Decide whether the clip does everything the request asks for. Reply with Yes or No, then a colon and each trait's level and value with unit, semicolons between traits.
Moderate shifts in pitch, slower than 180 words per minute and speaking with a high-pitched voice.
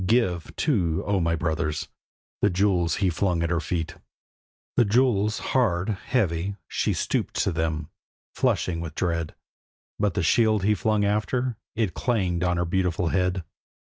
No: average, 4.0 semitones; average, 150 wpm; very low, 90 Hz